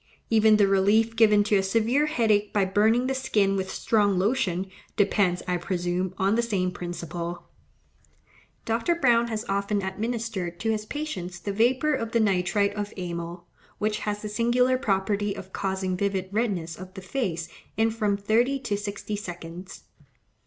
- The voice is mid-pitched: No, high, 205 Hz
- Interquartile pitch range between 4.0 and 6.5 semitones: No, average, 3.1 semitones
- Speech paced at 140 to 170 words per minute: Yes, average, 160 wpm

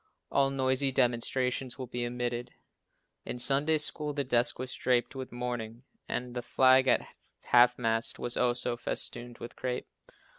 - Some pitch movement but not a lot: No, narrow, 1.5 semitones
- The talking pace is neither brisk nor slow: Yes, average, 150 wpm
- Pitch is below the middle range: Yes, low, 125 Hz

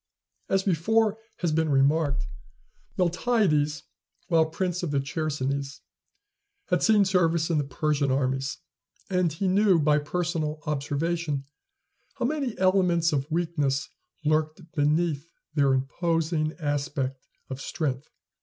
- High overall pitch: No, medium, 155 Hz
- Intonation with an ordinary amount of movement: Yes, average, 3.5 semitones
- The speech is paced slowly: Yes, slow, 115 wpm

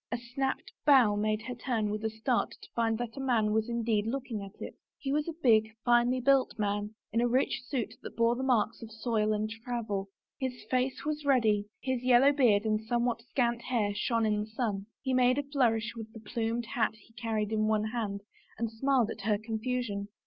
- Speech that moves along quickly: Yes, fast, 210 wpm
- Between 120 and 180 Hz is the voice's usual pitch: No, high, 230 Hz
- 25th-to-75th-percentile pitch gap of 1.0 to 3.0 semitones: Yes, average, 2.7 semitones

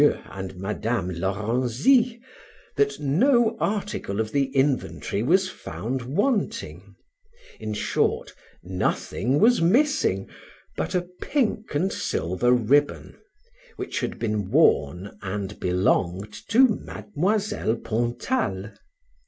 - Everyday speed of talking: No, slow, 100 wpm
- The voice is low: Yes, low, 125 Hz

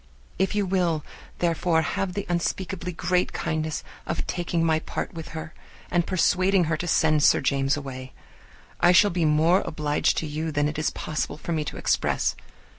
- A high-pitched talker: No, medium, 165 Hz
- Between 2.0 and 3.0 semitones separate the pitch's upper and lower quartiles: Yes, narrow, 2.6 semitones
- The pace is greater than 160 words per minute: Yes, average, 180 wpm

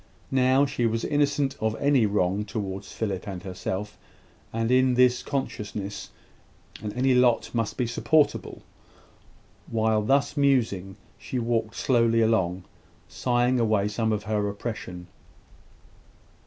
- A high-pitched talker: No, low, 115 Hz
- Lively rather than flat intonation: No, average, 3.5 semitones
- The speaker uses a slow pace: Yes, slow, 120 wpm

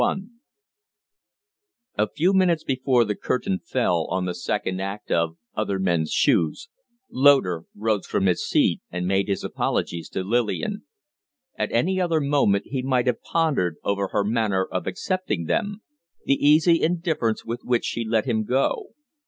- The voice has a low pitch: Yes, low, 115 Hz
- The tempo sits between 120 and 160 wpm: Yes, average, 155 wpm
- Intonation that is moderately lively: No, wide, 8.0 semitones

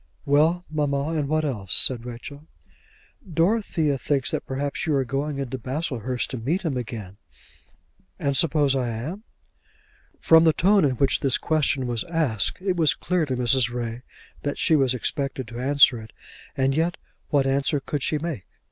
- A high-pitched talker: No, medium, 140 Hz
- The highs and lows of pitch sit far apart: No, average, 3.7 semitones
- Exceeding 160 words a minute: Yes, average, 170 wpm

